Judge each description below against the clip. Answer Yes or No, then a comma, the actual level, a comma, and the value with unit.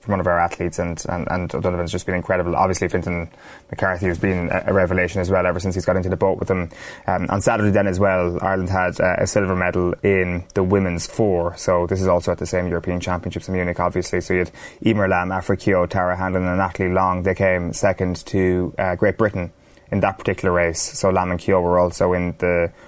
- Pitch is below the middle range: Yes, very low, 90 Hz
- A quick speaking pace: Yes, fast, 235 wpm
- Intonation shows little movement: Yes, narrow, 1.3 semitones